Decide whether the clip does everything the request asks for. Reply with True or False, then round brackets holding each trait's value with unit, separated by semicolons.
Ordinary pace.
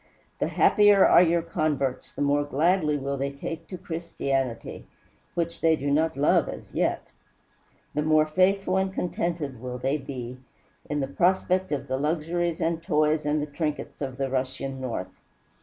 True (170 wpm)